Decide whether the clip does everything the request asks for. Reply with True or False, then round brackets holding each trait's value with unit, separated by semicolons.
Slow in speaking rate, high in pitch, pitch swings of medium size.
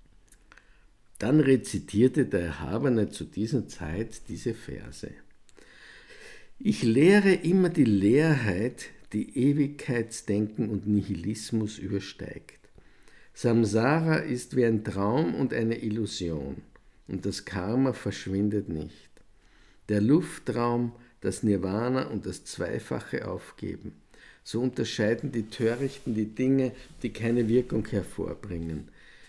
False (100 wpm; 110 Hz; 4.0 semitones)